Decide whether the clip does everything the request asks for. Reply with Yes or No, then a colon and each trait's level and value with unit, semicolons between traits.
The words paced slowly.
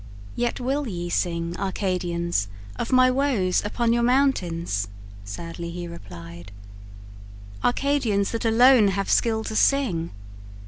Yes: slow, 120 wpm